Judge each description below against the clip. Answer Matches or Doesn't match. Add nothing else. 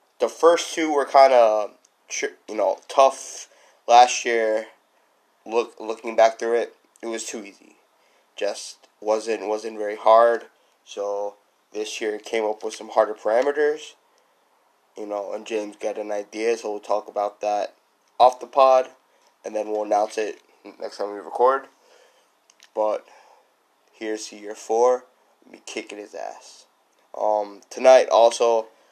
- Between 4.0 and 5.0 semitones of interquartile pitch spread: Doesn't match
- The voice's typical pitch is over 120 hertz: Doesn't match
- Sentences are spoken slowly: Doesn't match